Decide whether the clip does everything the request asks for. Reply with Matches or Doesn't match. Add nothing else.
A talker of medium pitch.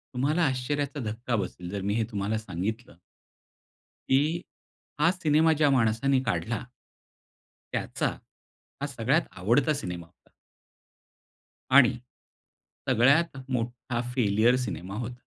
Doesn't match